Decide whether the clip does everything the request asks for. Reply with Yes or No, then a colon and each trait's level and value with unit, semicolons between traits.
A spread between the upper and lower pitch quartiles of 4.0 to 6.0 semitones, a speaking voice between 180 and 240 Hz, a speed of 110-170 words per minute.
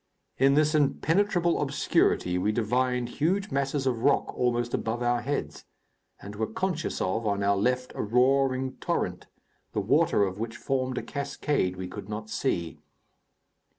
No: average, 4.5 semitones; low, 125 Hz; average, 150 wpm